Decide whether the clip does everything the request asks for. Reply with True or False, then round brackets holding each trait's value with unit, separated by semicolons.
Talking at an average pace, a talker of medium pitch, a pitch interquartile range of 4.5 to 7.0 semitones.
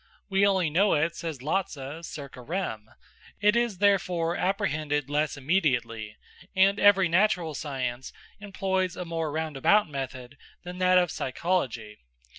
False (130 wpm; 165 Hz; 5.5 semitones)